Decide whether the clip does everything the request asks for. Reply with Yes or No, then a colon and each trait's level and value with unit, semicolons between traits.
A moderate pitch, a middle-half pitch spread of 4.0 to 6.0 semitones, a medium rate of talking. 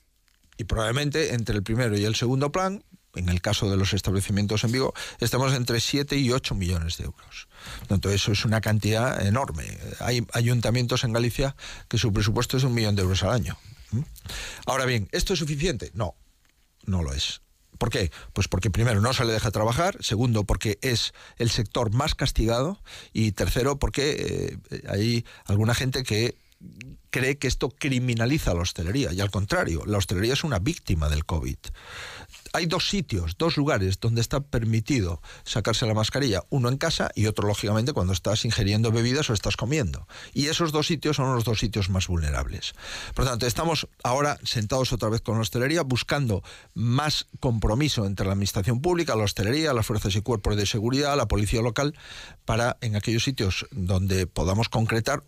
No: low, 115 Hz; average, 4.3 semitones; average, 180 wpm